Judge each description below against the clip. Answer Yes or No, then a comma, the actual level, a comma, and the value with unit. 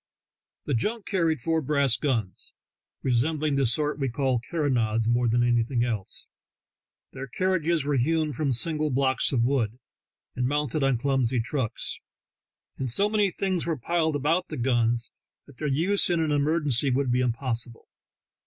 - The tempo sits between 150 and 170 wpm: Yes, average, 155 wpm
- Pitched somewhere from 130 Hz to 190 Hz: Yes, low, 135 Hz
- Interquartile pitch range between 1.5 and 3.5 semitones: No, average, 4.5 semitones